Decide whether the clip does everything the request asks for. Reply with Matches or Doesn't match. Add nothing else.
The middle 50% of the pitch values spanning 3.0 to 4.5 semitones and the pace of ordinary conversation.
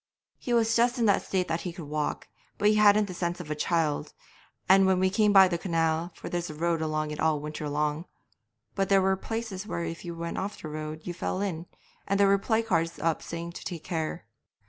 Doesn't match